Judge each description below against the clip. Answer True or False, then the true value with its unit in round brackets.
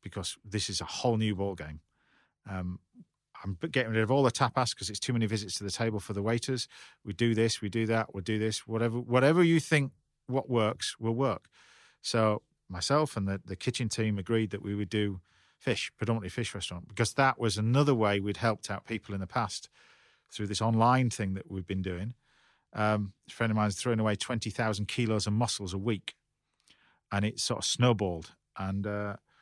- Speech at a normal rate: False (210 wpm)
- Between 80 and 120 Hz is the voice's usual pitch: True (110 Hz)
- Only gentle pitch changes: False (3.2 semitones)